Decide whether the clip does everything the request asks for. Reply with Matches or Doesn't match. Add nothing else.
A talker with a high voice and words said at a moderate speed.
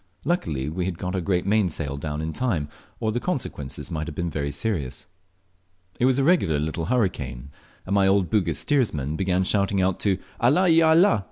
Doesn't match